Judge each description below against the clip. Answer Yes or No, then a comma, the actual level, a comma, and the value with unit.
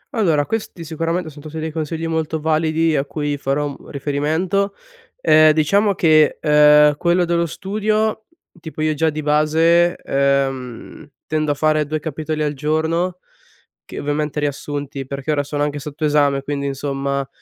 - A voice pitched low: No, medium, 155 Hz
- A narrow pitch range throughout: Yes, narrow, 2.0 semitones